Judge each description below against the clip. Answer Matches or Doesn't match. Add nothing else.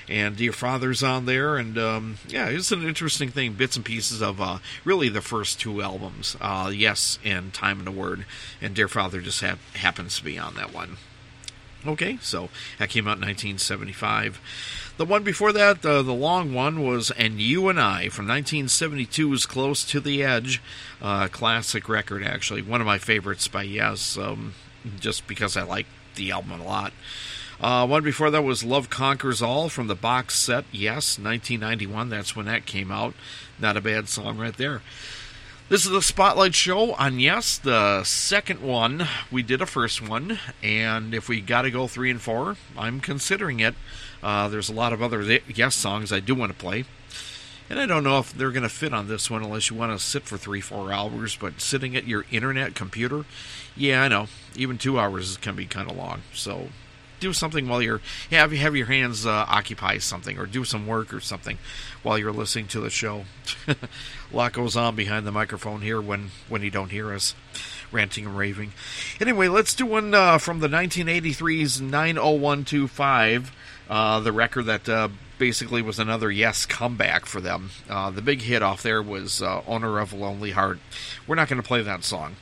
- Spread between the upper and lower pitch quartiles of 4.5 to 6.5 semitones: Doesn't match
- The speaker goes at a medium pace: Matches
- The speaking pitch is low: Matches